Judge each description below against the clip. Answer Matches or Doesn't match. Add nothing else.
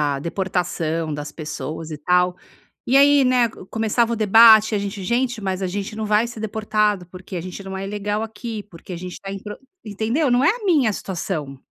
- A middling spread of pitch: Matches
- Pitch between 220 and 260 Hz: Doesn't match